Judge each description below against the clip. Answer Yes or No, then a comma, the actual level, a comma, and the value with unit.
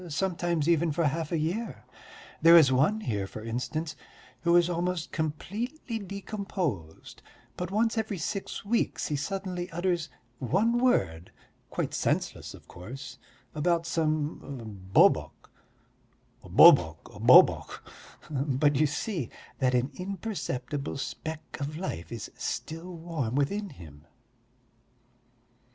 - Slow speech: Yes, slow, 115 wpm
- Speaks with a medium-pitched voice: Yes, medium, 160 Hz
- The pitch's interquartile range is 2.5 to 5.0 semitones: No, wide, 5.4 semitones